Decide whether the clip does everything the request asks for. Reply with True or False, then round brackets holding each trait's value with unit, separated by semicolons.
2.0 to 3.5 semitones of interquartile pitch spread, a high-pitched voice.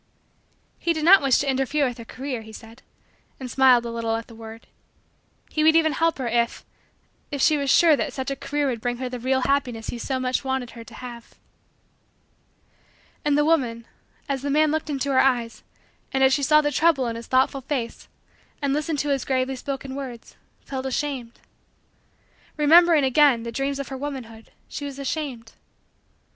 True (3.1 semitones; 265 Hz)